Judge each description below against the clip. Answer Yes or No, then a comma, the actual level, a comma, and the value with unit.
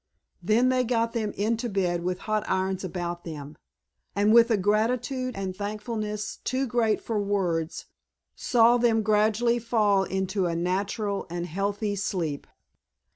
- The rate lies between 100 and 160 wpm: Yes, average, 140 wpm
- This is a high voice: Yes, high, 205 Hz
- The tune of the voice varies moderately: Yes, average, 3.4 semitones